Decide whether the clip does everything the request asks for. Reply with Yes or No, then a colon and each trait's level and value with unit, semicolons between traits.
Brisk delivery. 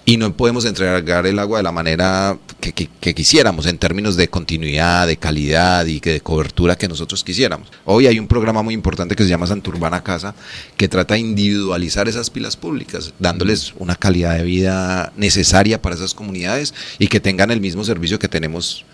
Yes: fast, 195 wpm